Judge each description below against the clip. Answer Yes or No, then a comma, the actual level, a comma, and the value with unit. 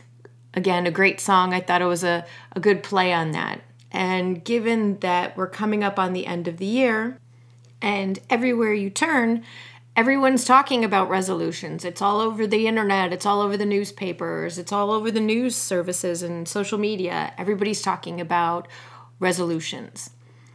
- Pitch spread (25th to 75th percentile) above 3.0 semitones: Yes, average, 3.4 semitones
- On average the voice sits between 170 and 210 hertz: Yes, high, 190 Hz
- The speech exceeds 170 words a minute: No, average, 165 wpm